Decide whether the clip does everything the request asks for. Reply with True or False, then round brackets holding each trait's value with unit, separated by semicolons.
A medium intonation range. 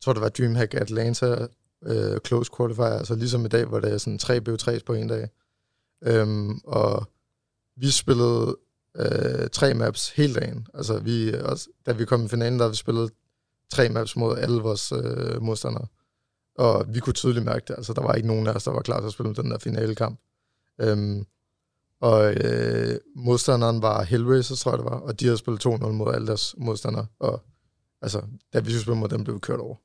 False (1.9 semitones)